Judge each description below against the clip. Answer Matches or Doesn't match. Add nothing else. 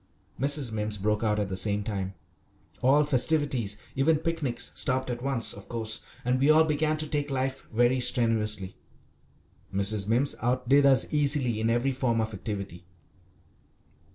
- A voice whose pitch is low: Matches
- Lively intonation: Doesn't match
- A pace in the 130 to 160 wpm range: Matches